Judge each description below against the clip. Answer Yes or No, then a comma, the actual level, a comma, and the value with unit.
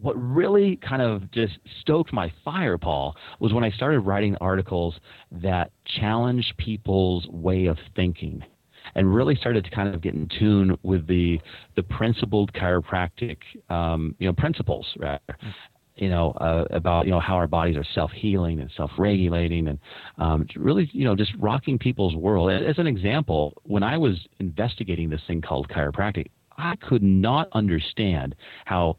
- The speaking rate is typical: Yes, average, 170 wpm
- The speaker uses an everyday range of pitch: Yes, average, 4.3 semitones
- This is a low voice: Yes, very low, 95 Hz